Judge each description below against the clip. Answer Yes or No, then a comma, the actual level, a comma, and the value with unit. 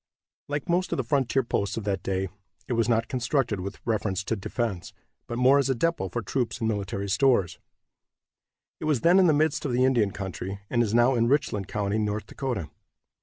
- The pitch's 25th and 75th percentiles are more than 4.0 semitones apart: Yes, average, 4.9 semitones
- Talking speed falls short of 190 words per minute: No, fast, 205 wpm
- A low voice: Yes, low, 115 Hz